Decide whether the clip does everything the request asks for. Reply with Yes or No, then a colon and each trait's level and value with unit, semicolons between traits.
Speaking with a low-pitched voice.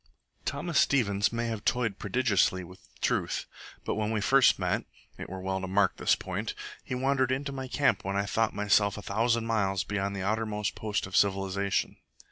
Yes: low, 105 Hz